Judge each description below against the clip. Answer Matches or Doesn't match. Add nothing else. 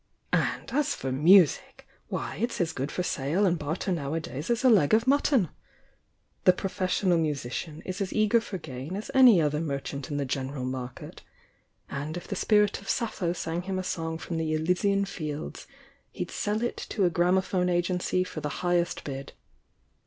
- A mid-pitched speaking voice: Matches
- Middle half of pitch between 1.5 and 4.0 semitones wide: Doesn't match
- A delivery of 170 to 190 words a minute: Matches